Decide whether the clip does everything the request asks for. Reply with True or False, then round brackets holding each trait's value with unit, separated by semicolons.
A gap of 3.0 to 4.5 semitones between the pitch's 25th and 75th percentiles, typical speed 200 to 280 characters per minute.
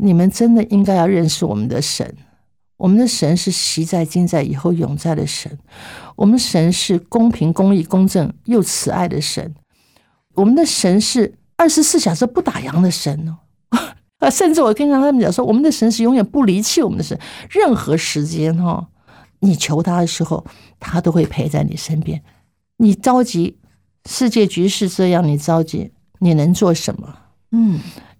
False (5.6 semitones; 255 characters per minute)